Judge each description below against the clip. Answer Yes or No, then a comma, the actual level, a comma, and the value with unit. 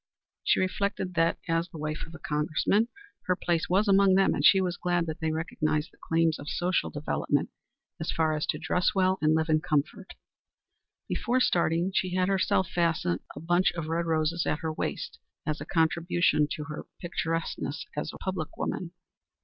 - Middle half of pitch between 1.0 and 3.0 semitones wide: Yes, narrow, 2.6 semitones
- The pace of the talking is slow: No, average, 185 wpm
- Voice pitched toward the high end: No, medium, 165 Hz